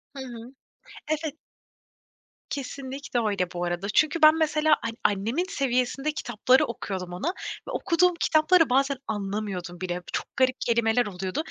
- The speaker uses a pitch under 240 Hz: No, high, 245 Hz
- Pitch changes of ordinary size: No, wide, 7.0 semitones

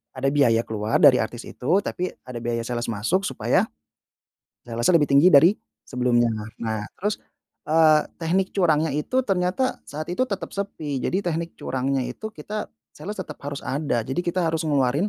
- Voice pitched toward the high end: No, medium, 150 Hz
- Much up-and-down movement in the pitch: Yes, wide, 6.3 semitones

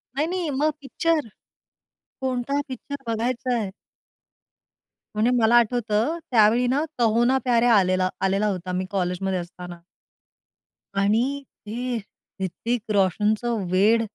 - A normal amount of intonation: Yes, average, 4.2 semitones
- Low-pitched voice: No, high, 225 Hz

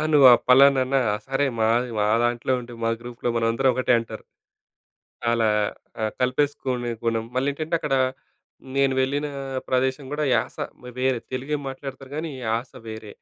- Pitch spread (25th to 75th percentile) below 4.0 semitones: Yes, narrow, 2.6 semitones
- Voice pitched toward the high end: No, low, 130 Hz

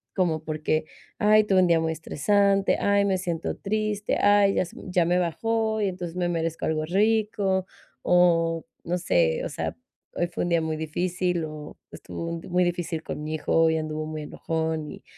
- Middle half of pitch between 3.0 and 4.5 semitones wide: Yes, average, 3.5 semitones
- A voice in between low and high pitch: Yes, medium, 175 Hz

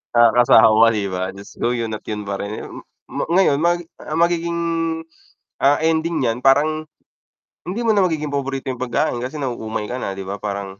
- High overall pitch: No, low, 130 Hz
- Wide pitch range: Yes, wide, 6.5 semitones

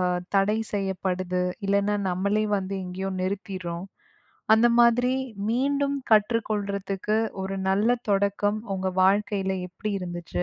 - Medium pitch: No, high, 200 Hz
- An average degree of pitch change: No, narrow, 2.2 semitones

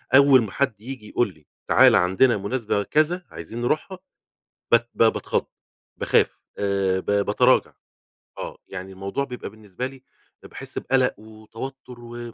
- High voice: No, low, 115 Hz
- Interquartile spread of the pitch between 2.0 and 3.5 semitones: No, average, 4.6 semitones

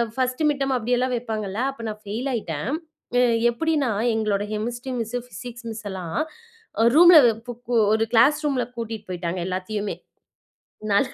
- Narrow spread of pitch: No, average, 3.4 semitones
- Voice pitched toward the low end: No, high, 230 Hz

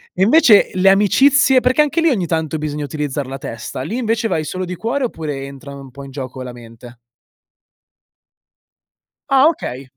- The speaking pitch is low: No, medium, 160 Hz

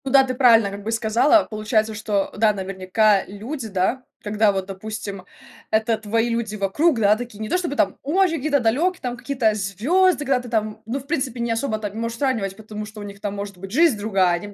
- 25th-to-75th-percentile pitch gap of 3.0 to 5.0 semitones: Yes, average, 3.9 semitones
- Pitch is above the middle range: Yes, high, 220 Hz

